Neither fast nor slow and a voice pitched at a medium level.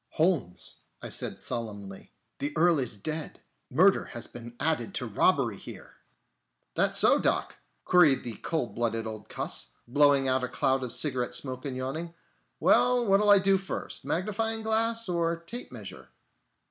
Yes: average, 155 wpm; medium, 145 Hz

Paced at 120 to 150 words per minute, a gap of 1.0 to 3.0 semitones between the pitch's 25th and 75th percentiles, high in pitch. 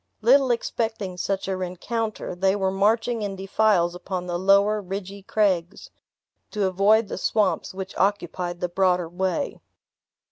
Yes: average, 140 wpm; narrow, 2.6 semitones; high, 195 Hz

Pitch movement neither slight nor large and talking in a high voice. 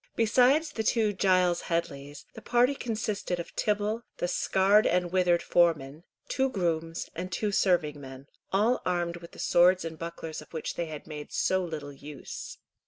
No: average, 4.2 semitones; medium, 175 Hz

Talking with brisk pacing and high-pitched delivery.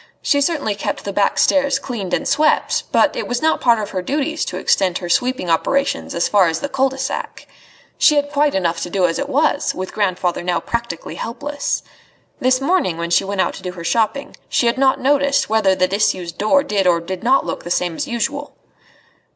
Yes: fast, 215 wpm; high, 230 Hz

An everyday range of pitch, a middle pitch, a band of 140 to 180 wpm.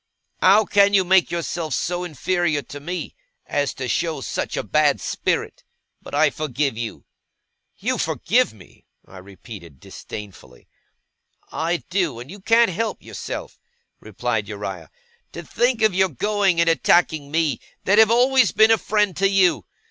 No: wide, 5.8 semitones; medium, 175 Hz; average, 155 wpm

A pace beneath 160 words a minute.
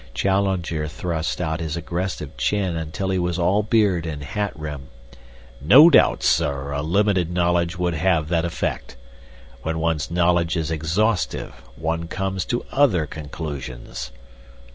Yes: average, 140 wpm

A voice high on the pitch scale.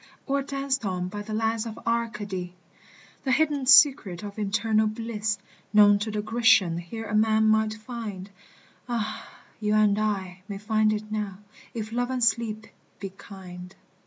Yes: high, 215 Hz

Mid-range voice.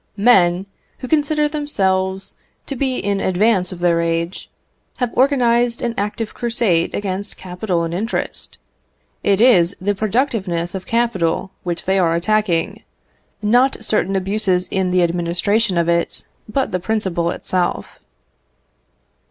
No: high, 195 Hz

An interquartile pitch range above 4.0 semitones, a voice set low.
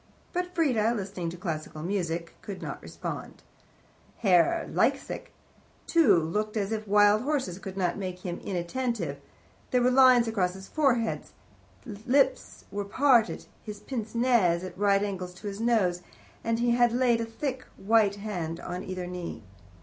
No: average, 4.8 semitones; high, 205 Hz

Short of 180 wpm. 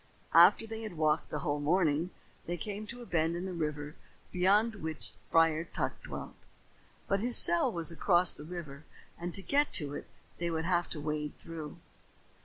No: average, 185 wpm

